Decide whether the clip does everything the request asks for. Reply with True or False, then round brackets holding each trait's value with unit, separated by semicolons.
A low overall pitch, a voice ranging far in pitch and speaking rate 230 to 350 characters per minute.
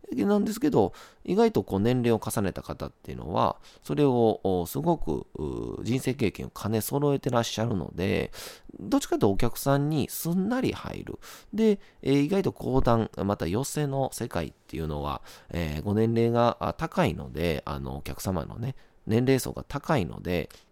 True (120 Hz; 7.2 semitones; 325 characters per minute)